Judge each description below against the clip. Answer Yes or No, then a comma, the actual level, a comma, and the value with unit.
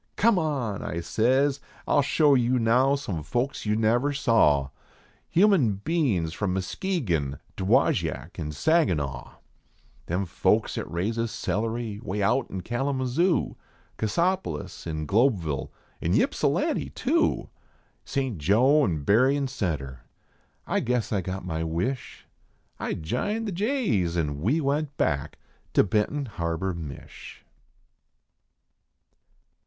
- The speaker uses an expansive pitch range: Yes, wide, 8.6 semitones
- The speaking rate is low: Yes, slow, 125 wpm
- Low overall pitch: Yes, low, 110 Hz